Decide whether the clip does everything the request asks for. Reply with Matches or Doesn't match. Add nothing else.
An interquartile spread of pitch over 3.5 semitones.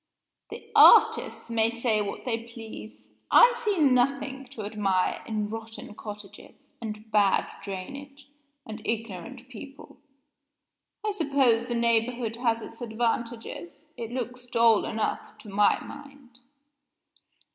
Doesn't match